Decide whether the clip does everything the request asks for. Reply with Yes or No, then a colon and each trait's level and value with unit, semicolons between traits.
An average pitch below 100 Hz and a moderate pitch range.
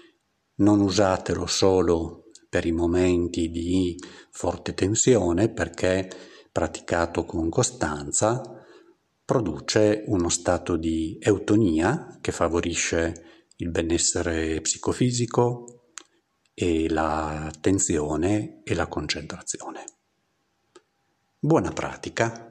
Yes: very low, 85 Hz; average, 4.1 semitones